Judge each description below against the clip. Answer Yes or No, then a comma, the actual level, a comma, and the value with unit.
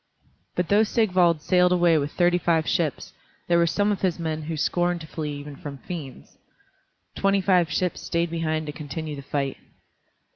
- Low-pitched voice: No, medium, 170 Hz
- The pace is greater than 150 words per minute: Yes, average, 180 wpm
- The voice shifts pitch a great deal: No, average, 2.9 semitones